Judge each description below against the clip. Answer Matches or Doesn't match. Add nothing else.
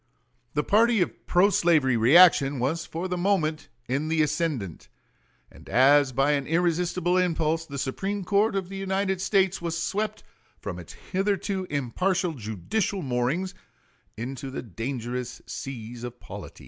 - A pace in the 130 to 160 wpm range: Matches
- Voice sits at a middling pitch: Matches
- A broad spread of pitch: Matches